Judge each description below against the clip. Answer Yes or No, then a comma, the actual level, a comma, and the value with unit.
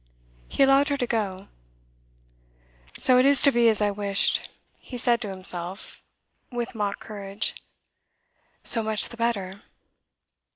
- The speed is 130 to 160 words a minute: Yes, slow, 135 wpm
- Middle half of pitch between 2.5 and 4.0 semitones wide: Yes, average, 3.5 semitones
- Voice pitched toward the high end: Yes, high, 220 Hz